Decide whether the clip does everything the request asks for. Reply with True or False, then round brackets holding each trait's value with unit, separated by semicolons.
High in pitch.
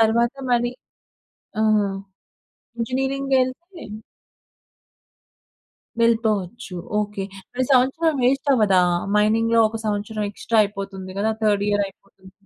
True (225 Hz)